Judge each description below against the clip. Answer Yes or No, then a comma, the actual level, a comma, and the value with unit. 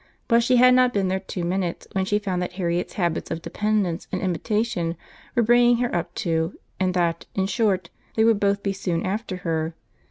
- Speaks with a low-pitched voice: No, high, 190 Hz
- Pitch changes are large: No, average, 3.7 semitones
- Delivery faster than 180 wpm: Yes, average, 200 wpm